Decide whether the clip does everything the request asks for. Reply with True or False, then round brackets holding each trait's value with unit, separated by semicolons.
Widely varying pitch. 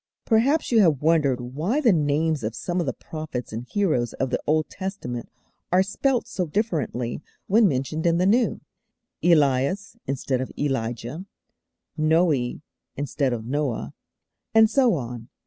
True (6.8 semitones)